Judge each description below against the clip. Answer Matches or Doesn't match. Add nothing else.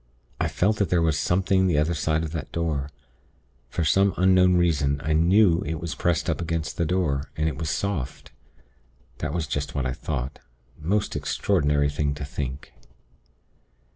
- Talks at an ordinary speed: Matches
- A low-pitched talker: Matches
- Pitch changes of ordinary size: Matches